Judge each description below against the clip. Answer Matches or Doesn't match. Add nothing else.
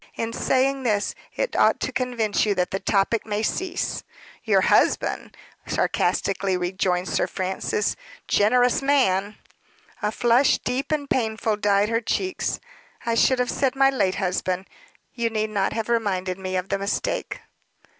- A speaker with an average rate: Matches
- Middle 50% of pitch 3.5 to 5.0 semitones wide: Matches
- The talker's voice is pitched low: Doesn't match